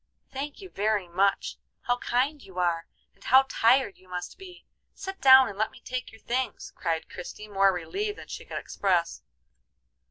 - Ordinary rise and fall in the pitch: No, wide, 6.4 semitones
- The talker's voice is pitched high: Yes, high, 220 Hz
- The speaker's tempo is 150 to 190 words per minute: Yes, average, 180 wpm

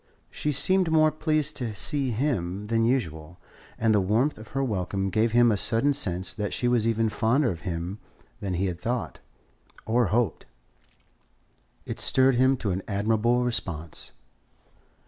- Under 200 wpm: Yes, average, 160 wpm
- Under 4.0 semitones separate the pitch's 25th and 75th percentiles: No, average, 5.0 semitones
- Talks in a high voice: No, low, 115 Hz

